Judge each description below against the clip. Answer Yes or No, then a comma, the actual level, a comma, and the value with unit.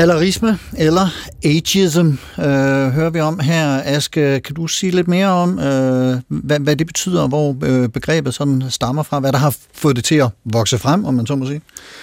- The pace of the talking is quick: No, average, 195 wpm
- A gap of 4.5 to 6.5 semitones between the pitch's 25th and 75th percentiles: No, average, 3.3 semitones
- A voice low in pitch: No, medium, 145 Hz